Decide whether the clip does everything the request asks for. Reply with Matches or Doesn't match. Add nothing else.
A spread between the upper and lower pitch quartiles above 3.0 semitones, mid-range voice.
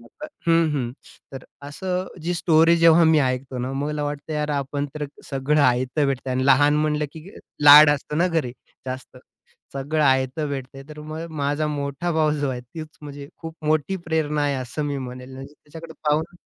Doesn't match